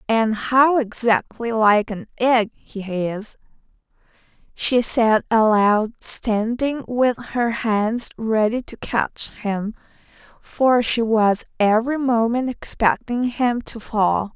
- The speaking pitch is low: No, high, 225 Hz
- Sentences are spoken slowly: Yes, slow, 115 wpm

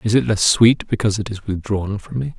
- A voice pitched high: No, low, 105 Hz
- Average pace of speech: No, fast, 250 wpm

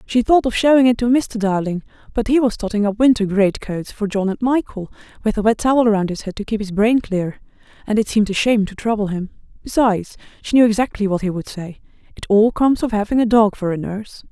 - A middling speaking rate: No, fast, 245 wpm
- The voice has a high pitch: Yes, high, 215 Hz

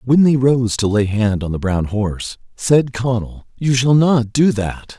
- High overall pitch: No, low, 120 Hz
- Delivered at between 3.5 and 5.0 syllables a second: Yes, 4.2 syllables/s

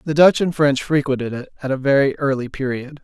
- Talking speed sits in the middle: No, fast, 220 wpm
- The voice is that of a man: Yes, male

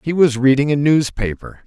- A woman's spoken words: No, male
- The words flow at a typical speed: Yes, average, 180 wpm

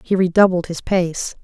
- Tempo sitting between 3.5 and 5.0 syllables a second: Yes, 4.7 syllables/s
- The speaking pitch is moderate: Yes, medium, 180 Hz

